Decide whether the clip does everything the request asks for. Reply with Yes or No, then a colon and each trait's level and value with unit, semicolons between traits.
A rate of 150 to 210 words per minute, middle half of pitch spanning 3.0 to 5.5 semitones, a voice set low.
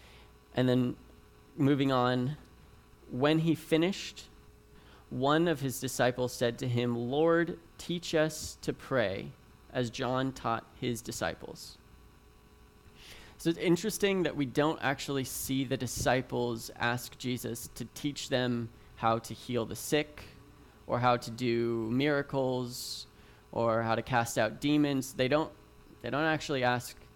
No: slow, 135 wpm; average, 3.7 semitones; low, 125 Hz